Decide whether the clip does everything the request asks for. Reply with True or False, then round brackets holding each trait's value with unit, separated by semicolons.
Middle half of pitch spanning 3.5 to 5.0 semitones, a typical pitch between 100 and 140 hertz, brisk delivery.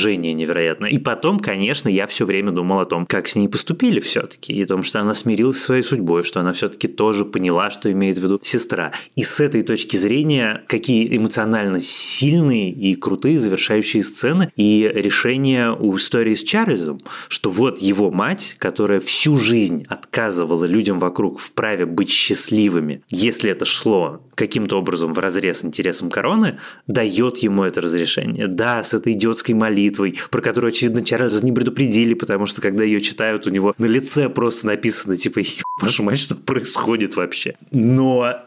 True (3.8 semitones; 110 Hz; 165 wpm)